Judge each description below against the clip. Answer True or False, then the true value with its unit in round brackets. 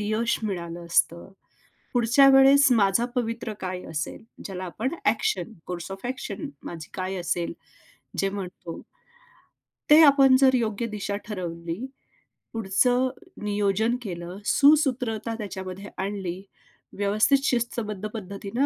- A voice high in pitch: True (210 Hz)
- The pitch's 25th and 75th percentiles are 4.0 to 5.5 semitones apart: True (4.5 semitones)